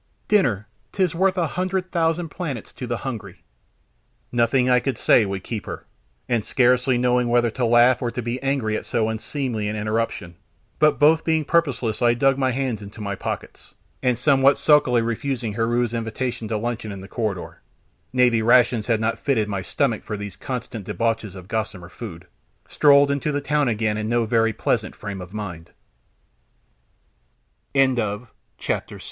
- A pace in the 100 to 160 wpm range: No, average, 175 wpm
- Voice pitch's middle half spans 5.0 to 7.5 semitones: No, average, 3.8 semitones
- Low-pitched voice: Yes, low, 120 Hz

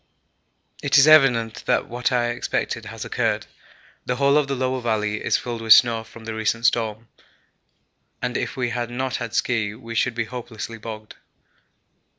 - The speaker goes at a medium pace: Yes, average, 170 wpm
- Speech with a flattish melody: Yes, narrow, 2.0 semitones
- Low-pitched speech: Yes, low, 120 Hz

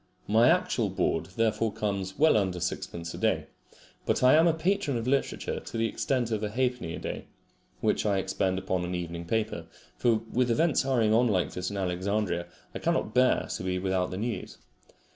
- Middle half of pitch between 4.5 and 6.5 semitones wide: Yes, average, 4.9 semitones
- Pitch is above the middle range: No, low, 105 Hz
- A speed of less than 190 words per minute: No, average, 195 wpm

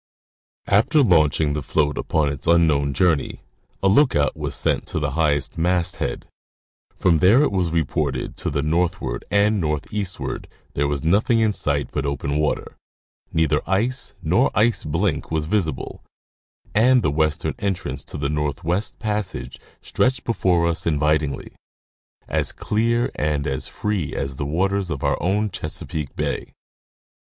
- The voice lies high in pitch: No, very low, 80 Hz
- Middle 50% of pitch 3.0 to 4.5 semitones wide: No, average, 5.3 semitones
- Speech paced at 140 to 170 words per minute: Yes, average, 145 wpm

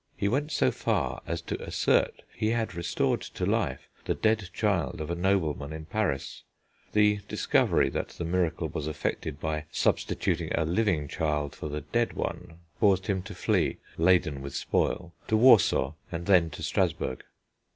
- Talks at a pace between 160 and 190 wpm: Yes, average, 165 wpm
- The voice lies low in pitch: Yes, very low, 85 Hz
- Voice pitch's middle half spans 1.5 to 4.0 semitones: No, average, 4.8 semitones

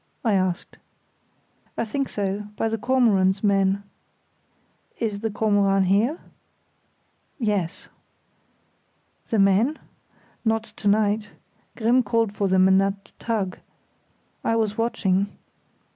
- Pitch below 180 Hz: No, high, 205 Hz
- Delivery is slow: Yes, slow, 110 wpm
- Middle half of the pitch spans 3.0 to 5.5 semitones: No, narrow, 2.4 semitones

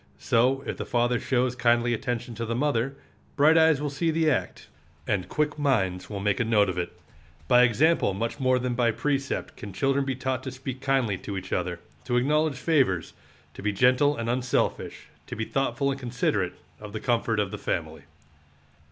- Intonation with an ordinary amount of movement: Yes, average, 3.8 semitones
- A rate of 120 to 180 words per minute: No, average, 195 wpm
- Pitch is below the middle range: Yes, low, 125 Hz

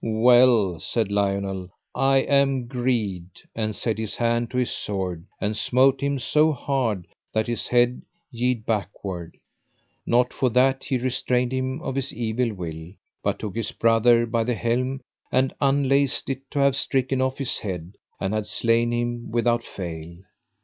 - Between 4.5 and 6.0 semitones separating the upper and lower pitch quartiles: No, average, 3.6 semitones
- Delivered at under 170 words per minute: Yes, average, 160 wpm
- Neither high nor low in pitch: No, low, 120 Hz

